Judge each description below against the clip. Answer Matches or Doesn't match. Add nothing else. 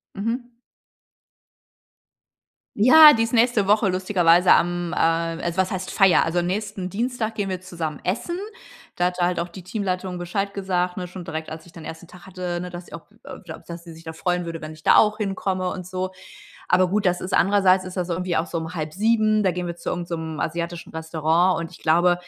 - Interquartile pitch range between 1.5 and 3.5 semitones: Matches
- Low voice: Doesn't match